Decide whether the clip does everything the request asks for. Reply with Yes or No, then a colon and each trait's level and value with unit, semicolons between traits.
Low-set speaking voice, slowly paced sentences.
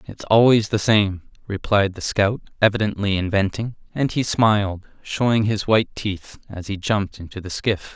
No: low, 100 Hz; average, 165 wpm